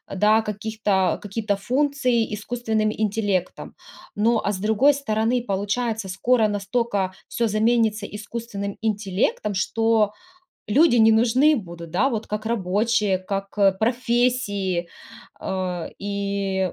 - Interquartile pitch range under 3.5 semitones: Yes, average, 2.7 semitones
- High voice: Yes, high, 215 Hz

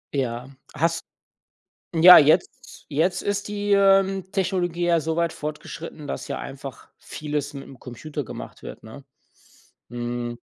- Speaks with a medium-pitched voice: Yes, medium, 160 Hz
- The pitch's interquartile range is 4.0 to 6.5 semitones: Yes, average, 4.6 semitones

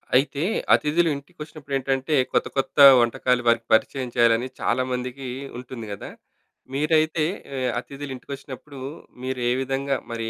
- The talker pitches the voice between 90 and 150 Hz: Yes, low, 135 Hz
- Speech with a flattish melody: Yes, narrow, 2.3 semitones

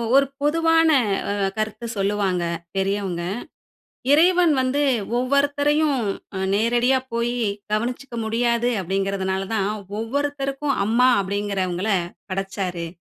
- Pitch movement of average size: No, wide, 6.1 semitones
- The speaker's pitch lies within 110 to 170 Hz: No, high, 235 Hz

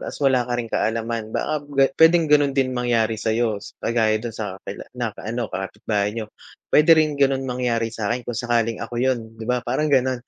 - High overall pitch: No, low, 120 Hz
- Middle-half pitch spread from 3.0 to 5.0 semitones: No, narrow, 2.6 semitones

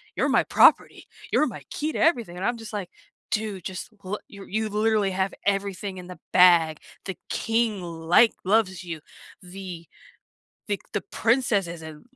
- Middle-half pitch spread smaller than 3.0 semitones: No, average, 3.4 semitones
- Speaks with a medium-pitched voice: No, high, 195 Hz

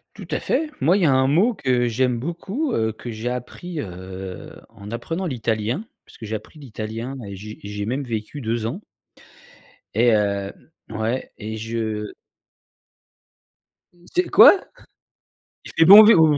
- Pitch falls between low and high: No, low, 120 Hz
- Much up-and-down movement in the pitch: Yes, wide, 6.1 semitones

